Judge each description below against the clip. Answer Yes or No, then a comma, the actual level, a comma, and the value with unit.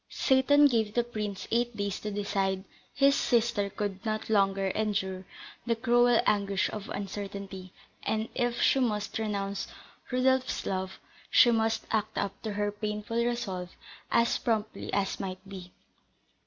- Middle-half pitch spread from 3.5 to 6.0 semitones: No, average, 3.0 semitones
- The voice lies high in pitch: Yes, high, 210 Hz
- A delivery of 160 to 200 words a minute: No, average, 140 wpm